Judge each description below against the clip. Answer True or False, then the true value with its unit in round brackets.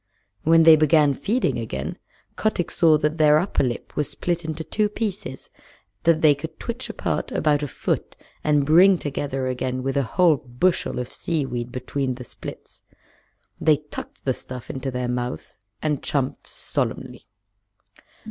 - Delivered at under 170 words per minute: True (155 wpm)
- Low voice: False (150 Hz)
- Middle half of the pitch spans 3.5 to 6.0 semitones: True (4.0 semitones)